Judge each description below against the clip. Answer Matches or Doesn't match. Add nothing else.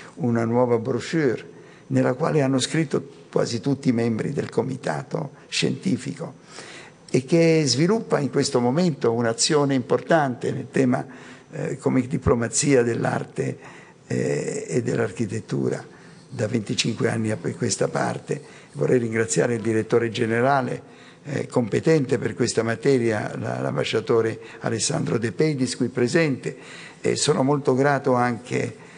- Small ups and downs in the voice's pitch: Doesn't match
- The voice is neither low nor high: Doesn't match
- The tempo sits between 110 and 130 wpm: Matches